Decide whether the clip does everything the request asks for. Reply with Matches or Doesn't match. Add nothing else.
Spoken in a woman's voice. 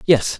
Doesn't match